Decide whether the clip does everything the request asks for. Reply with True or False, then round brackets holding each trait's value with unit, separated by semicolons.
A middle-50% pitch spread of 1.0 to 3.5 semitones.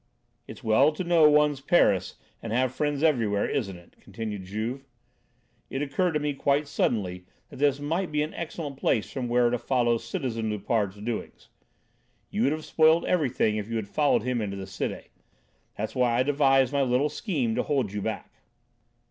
False (5.0 semitones)